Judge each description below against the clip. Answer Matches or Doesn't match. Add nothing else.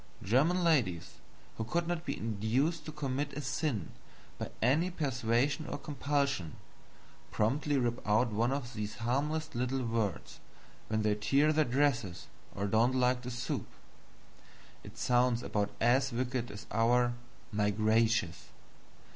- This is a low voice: Matches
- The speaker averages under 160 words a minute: Matches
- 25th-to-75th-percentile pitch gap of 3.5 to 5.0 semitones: Matches